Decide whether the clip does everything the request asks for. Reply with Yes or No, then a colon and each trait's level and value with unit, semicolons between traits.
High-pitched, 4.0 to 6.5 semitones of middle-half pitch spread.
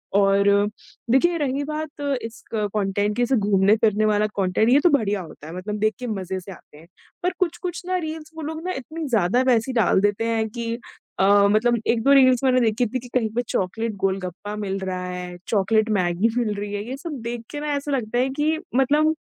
Yes: high, 225 Hz; average, 5.0 semitones